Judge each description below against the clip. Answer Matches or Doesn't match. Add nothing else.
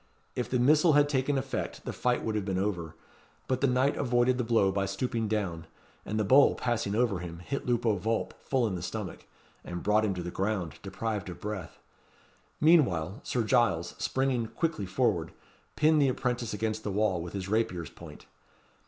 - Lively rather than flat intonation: Doesn't match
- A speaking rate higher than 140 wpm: Matches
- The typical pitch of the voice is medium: Doesn't match